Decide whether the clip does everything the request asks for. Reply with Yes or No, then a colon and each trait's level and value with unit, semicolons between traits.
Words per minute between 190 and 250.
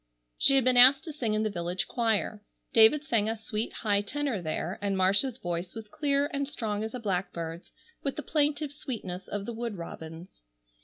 Yes: average, 195 wpm